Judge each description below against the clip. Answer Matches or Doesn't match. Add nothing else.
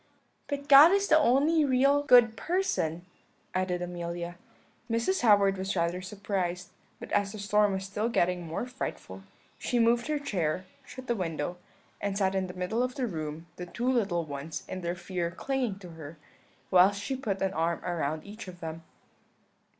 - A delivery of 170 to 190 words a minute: Matches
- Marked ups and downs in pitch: Matches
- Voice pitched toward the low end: Doesn't match